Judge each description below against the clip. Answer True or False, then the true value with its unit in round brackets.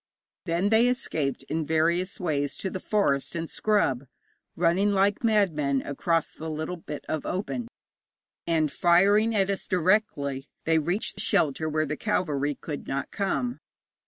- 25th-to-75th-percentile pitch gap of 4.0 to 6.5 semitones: True (5.0 semitones)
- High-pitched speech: False (170 Hz)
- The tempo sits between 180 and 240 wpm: False (145 wpm)